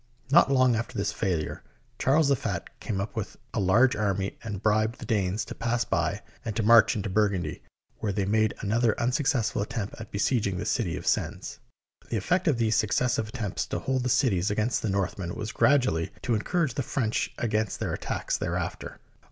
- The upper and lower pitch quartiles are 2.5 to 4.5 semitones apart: Yes, average, 3.5 semitones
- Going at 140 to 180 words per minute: No, average, 195 wpm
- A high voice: No, low, 110 Hz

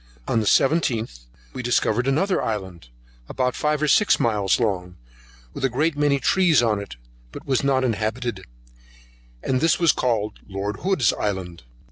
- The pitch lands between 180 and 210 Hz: No, low, 120 Hz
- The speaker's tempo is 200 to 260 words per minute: No, average, 150 wpm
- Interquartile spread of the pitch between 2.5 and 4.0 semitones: No, average, 5.3 semitones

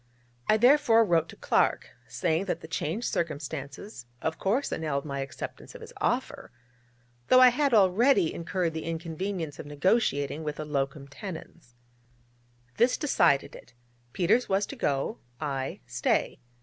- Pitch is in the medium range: Yes, medium, 165 Hz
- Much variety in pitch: Yes, wide, 6.6 semitones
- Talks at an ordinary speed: Yes, average, 145 wpm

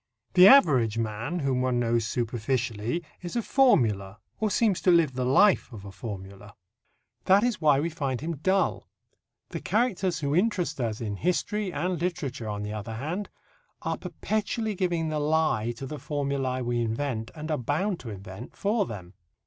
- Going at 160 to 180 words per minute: Yes, average, 175 wpm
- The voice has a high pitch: No, medium, 140 Hz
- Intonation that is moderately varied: No, wide, 7.7 semitones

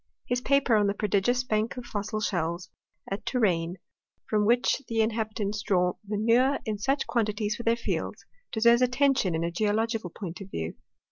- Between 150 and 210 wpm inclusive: Yes, average, 165 wpm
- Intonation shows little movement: No, average, 3.1 semitones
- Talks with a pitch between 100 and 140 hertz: No, high, 215 Hz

